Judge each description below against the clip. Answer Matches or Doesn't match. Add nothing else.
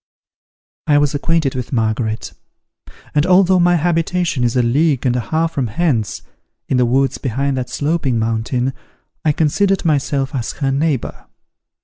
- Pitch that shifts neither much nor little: Matches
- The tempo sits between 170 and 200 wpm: Doesn't match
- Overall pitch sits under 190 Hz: Matches